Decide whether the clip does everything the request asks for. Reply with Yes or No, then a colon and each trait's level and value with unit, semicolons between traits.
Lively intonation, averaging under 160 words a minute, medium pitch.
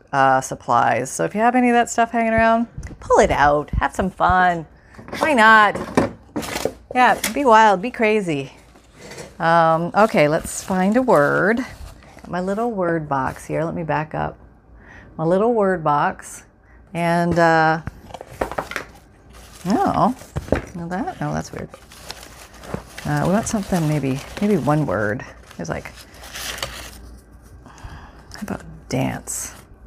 Yes: wide, 7.4 semitones; slow, 135 wpm; medium, 175 Hz